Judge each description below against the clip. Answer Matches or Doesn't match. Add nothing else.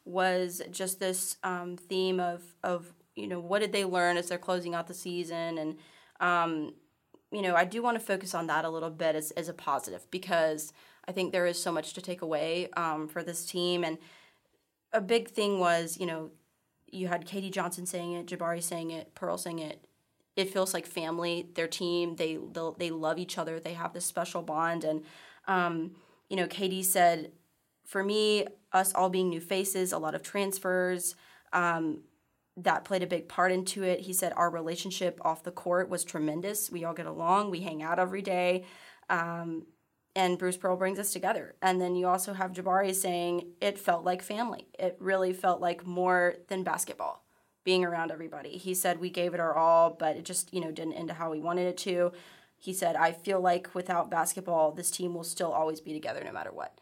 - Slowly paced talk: Doesn't match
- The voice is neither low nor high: Matches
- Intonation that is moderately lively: Doesn't match